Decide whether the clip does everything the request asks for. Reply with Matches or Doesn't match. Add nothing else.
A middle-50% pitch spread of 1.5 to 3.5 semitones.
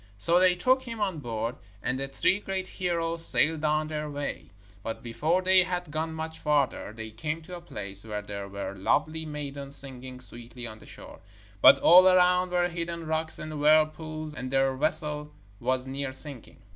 Doesn't match